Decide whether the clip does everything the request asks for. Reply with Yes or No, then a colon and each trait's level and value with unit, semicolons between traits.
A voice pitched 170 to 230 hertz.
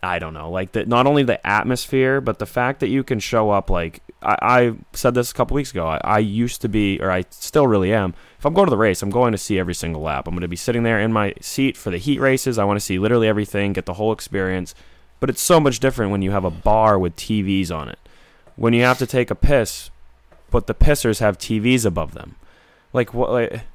No: low, 105 Hz